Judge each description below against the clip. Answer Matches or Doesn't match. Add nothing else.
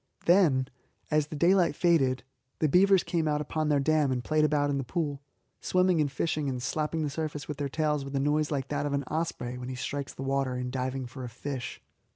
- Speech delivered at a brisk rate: Matches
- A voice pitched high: Doesn't match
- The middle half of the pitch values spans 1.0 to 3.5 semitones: Matches